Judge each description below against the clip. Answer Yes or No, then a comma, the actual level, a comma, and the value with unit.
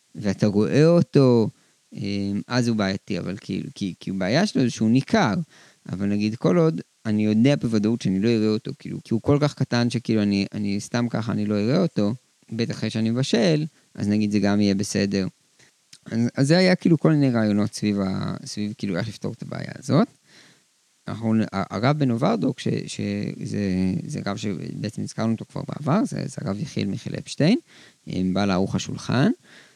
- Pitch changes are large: No, average, 3.7 semitones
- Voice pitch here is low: Yes, low, 110 Hz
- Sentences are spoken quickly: Yes, fast, 175 wpm